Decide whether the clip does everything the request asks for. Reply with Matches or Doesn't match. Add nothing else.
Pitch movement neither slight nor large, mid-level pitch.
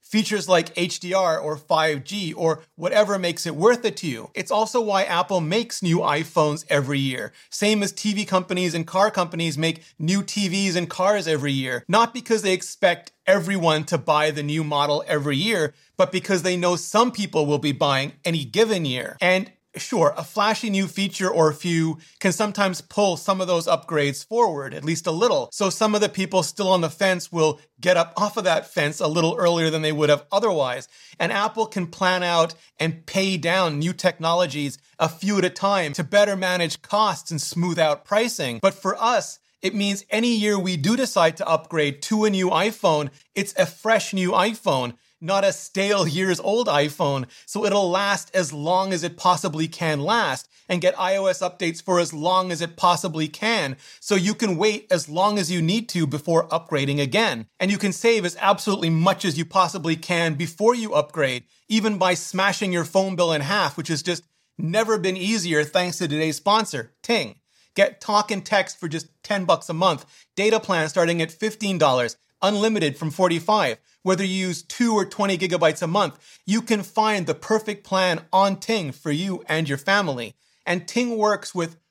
Matches